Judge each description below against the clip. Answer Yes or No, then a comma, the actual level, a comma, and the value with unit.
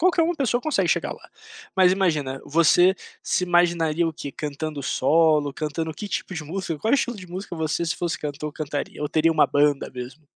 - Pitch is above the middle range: No, medium, 160 Hz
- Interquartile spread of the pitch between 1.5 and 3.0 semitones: No, average, 3.5 semitones